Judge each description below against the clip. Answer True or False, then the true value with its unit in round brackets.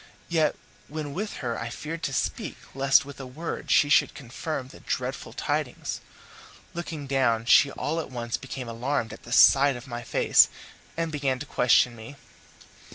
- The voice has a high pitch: False (135 Hz)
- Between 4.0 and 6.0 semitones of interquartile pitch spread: False (3.6 semitones)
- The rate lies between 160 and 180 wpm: True (170 wpm)